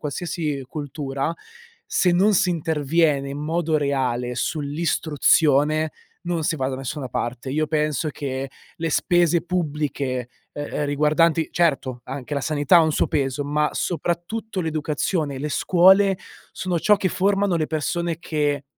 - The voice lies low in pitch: No, medium, 150 Hz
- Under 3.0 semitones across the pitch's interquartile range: No, average, 3.3 semitones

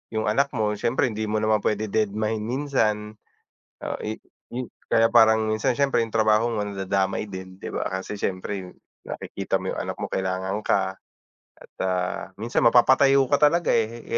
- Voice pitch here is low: Yes, low, 110 Hz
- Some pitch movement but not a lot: Yes, average, 3.0 semitones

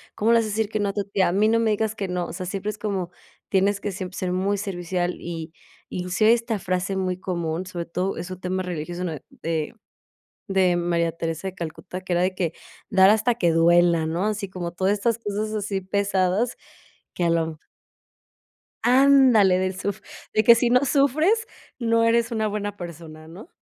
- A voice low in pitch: No, high, 190 Hz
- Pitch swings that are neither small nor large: Yes, average, 3.4 semitones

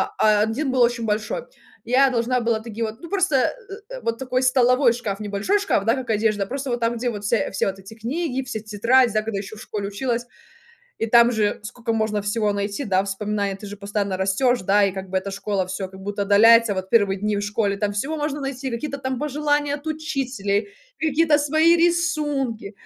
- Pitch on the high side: Yes, high, 230 Hz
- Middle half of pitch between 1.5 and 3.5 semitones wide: No, average, 4.6 semitones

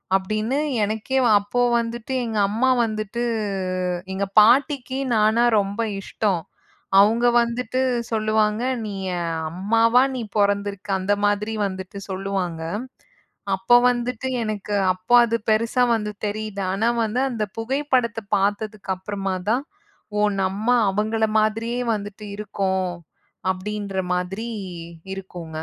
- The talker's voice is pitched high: Yes, high, 215 Hz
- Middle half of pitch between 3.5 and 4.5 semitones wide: No, average, 2.8 semitones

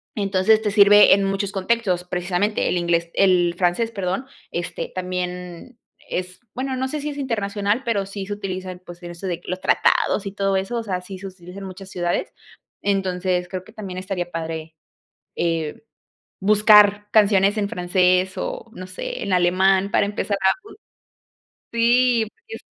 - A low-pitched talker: No, high, 190 Hz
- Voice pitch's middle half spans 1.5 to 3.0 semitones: Yes, narrow, 2.4 semitones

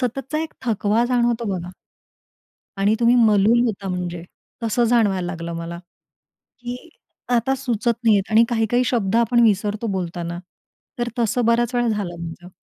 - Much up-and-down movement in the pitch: No, average, 4.1 semitones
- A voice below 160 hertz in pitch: No, high, 220 Hz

